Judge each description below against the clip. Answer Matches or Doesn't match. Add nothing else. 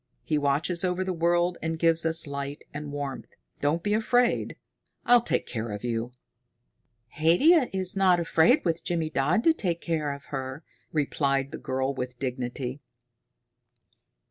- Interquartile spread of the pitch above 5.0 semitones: Doesn't match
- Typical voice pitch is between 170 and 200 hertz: Doesn't match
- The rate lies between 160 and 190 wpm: Doesn't match